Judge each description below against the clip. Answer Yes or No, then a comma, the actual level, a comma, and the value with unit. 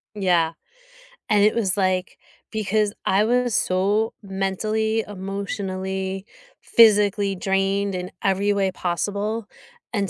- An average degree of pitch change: No, narrow, 1.7 semitones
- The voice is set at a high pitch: Yes, high, 200 Hz